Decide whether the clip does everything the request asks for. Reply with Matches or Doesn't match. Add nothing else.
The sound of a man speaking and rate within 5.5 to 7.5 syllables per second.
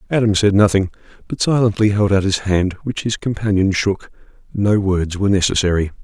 Matches